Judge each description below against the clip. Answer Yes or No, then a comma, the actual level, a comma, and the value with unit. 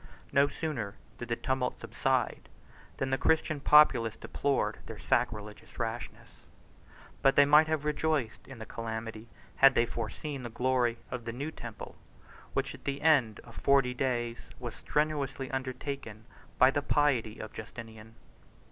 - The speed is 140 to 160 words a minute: Yes, average, 150 wpm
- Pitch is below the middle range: Yes, low, 125 Hz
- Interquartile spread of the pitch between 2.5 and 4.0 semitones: Yes, average, 3.7 semitones